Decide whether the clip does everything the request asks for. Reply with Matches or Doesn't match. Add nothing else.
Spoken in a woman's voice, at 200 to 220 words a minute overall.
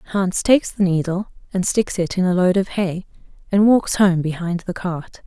Matches